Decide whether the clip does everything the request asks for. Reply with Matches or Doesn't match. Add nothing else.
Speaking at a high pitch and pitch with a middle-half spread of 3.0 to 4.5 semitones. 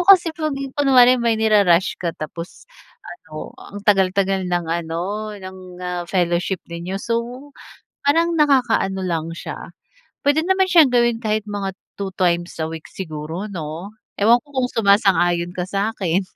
Doesn't match